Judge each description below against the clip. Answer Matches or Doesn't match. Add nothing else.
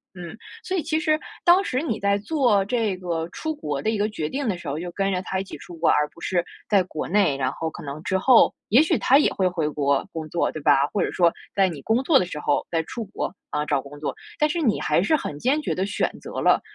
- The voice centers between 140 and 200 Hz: Matches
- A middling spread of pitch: Doesn't match